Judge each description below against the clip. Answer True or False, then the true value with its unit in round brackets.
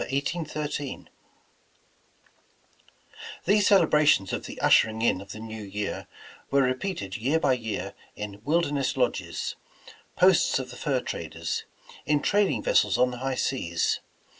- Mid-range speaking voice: False (130 Hz)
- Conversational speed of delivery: True (145 wpm)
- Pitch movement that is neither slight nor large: False (5.8 semitones)